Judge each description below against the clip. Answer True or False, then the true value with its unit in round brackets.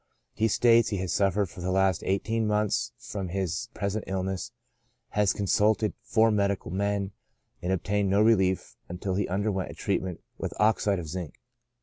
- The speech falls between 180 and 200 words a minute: False (160 wpm)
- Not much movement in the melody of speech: True (2.1 semitones)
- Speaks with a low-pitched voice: True (100 Hz)